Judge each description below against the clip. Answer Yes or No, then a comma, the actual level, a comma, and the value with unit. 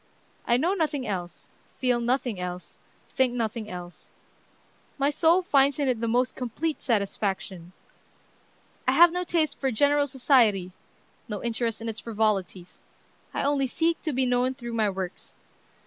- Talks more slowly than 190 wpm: Yes, average, 150 wpm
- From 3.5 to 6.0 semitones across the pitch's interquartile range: Yes, average, 5.0 semitones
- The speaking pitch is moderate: No, high, 245 Hz